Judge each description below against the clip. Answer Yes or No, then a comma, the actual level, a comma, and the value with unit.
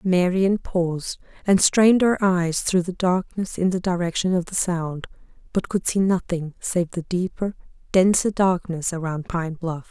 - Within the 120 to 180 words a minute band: Yes, average, 165 wpm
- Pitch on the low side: No, medium, 180 Hz